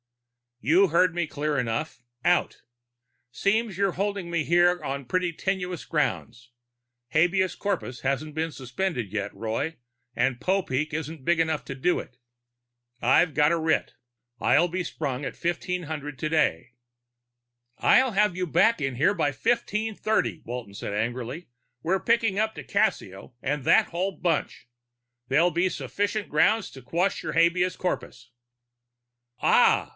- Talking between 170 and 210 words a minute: No, average, 140 wpm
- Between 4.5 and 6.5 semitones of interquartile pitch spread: Yes, average, 5.2 semitones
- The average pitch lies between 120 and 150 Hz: No, medium, 165 Hz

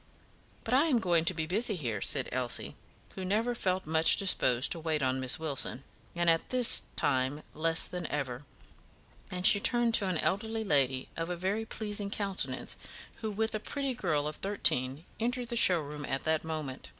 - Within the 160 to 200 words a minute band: Yes, average, 185 wpm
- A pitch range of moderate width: No, wide, 6.4 semitones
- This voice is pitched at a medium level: Yes, medium, 175 Hz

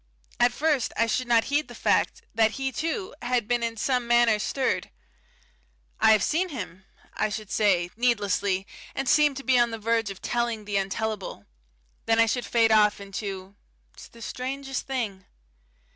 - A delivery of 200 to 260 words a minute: No, average, 175 wpm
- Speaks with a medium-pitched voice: No, high, 230 Hz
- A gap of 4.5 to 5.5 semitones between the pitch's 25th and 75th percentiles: No, average, 3.4 semitones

